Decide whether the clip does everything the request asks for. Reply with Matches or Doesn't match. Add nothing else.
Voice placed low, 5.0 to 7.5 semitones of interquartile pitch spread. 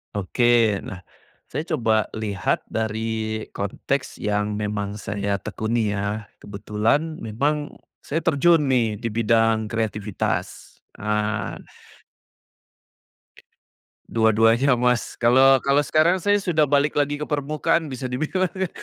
Matches